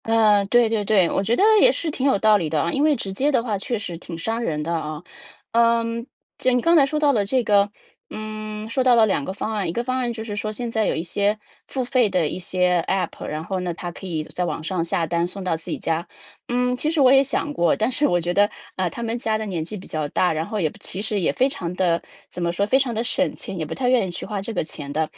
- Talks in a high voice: Yes, high, 210 Hz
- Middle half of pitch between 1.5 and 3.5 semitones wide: No, wide, 5.4 semitones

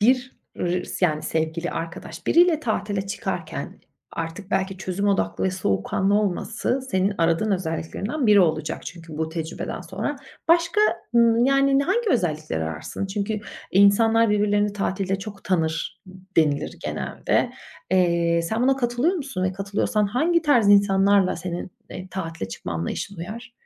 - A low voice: No, high, 195 Hz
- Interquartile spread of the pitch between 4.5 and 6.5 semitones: Yes, average, 5.0 semitones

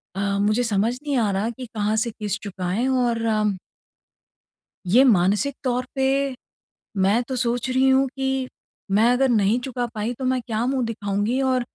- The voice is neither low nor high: No, high, 240 Hz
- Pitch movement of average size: Yes, average, 3.6 semitones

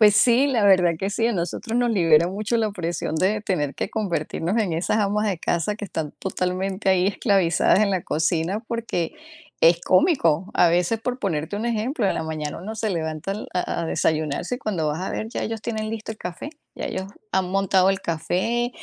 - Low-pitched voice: No, high, 190 Hz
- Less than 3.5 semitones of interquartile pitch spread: No, average, 4.3 semitones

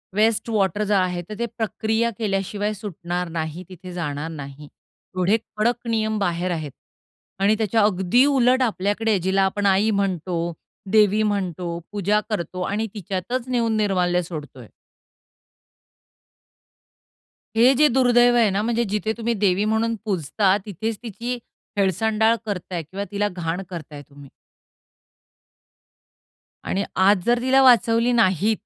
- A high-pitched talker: Yes, high, 205 Hz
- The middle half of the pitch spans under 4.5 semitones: Yes, average, 3.8 semitones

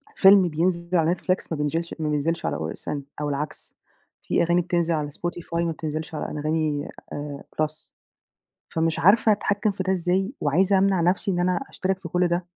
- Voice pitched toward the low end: No, medium, 170 Hz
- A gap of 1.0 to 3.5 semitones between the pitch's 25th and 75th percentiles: Yes, average, 3.1 semitones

